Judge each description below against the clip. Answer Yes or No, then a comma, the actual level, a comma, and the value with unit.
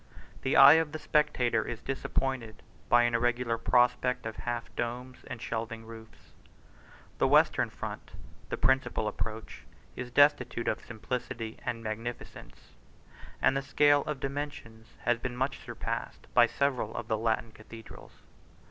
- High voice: No, low, 120 Hz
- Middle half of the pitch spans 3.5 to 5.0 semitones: No, average, 2.7 semitones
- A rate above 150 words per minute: No, average, 140 wpm